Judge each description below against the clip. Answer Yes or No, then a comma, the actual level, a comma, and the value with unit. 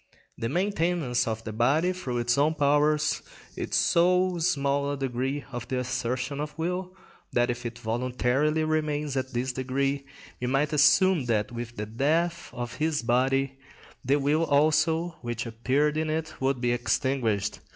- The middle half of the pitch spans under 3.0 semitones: No, average, 4.2 semitones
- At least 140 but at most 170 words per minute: Yes, average, 160 wpm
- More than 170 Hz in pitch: No, medium, 140 Hz